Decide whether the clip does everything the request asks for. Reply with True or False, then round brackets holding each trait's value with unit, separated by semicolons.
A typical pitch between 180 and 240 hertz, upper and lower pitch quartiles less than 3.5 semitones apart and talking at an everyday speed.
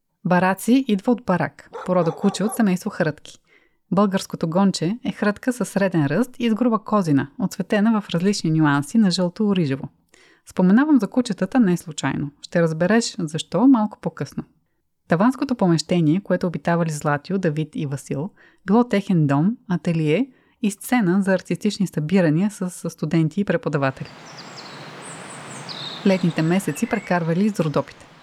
False (185 Hz; 4.2 semitones; 130 wpm)